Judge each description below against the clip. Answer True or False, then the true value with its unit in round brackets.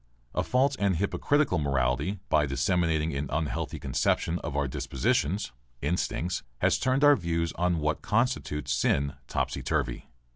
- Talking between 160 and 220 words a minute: False (140 wpm)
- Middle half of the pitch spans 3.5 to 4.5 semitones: False (5.6 semitones)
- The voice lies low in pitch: True (80 Hz)